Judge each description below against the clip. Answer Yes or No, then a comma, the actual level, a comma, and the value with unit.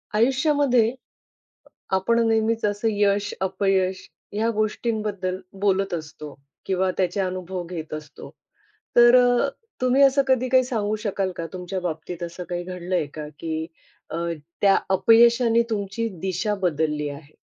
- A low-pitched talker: No, high, 195 Hz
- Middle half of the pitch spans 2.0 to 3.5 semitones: No, average, 4.3 semitones